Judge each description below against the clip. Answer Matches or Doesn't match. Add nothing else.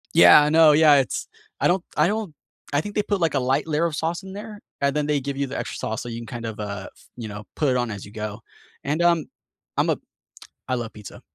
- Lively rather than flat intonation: Matches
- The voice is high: Doesn't match